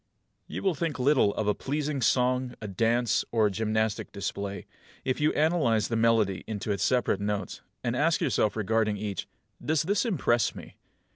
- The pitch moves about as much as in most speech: Yes, average, 4.5 semitones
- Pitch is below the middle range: Yes, low, 115 Hz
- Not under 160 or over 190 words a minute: Yes, average, 180 wpm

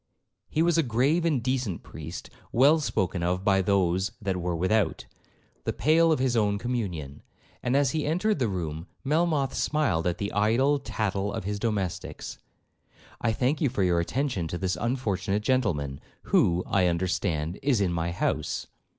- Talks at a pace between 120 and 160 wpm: No, average, 170 wpm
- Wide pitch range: Yes, wide, 6.7 semitones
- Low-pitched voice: Yes, low, 105 Hz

